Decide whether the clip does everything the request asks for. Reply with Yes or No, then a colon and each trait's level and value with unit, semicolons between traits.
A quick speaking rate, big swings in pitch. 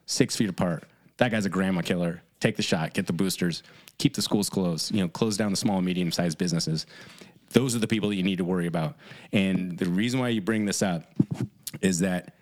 No: fast, 230 wpm; average, 3.4 semitones